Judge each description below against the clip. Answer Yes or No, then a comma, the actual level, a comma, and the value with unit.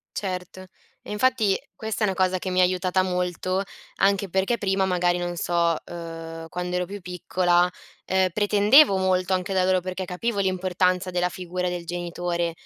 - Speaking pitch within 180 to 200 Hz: Yes, medium, 185 Hz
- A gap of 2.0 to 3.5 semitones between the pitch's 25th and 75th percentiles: No, narrow, 1.3 semitones